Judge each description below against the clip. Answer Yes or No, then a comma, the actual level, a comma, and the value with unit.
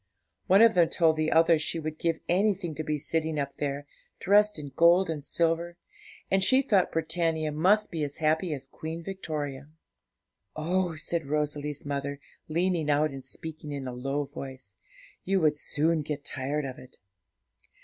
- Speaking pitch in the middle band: Yes, medium, 155 Hz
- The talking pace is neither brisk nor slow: Yes, average, 170 wpm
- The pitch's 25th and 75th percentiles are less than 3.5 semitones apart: Yes, average, 2.9 semitones